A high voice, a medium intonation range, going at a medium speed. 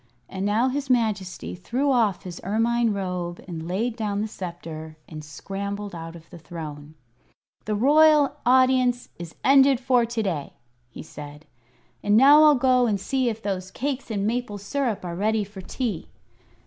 No: high, 210 Hz; wide, 5.8 semitones; average, 165 wpm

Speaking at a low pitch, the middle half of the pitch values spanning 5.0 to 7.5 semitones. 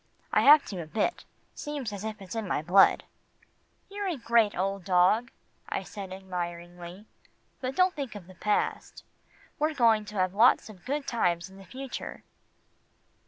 No: high, 210 Hz; wide, 5.5 semitones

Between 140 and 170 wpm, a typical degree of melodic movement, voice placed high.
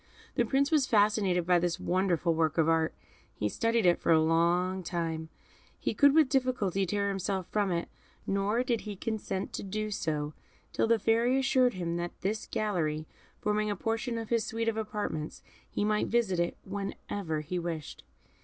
No: average, 180 wpm; average, 4.6 semitones; high, 195 Hz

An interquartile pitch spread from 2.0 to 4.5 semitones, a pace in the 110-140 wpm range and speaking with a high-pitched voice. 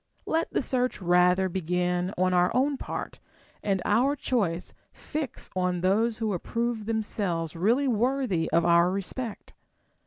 No: average, 5.1 semitones; slow, 135 wpm; high, 195 Hz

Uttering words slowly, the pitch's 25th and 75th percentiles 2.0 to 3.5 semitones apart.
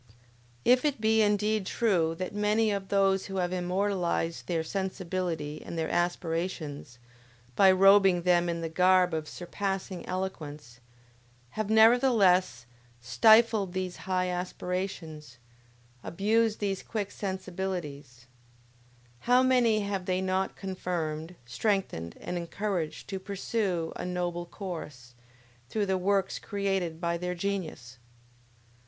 Yes: slow, 120 wpm; average, 3.0 semitones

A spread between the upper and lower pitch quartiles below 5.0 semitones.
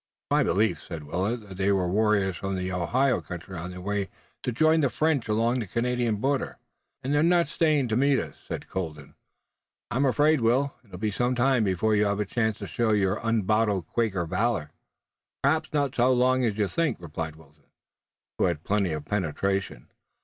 No: average, 5.3 semitones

